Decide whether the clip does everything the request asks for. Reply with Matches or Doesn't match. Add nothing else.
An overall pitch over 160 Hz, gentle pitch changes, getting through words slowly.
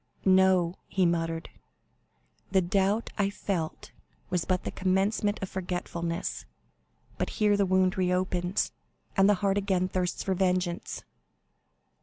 Matches